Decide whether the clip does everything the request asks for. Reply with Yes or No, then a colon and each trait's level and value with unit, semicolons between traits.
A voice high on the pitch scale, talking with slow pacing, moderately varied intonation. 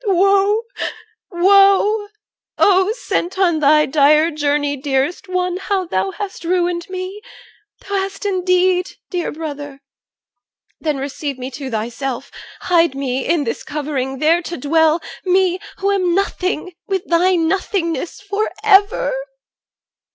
Yes: very high, 345 Hz; slow, 130 wpm; average, 4.8 semitones